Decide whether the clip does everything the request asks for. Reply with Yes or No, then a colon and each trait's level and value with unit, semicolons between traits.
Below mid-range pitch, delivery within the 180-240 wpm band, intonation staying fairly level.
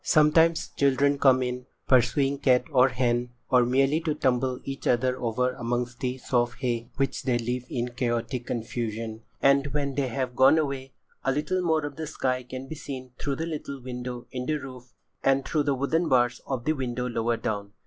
Yes: low, 130 Hz; average, 190 wpm; narrow, 2.3 semitones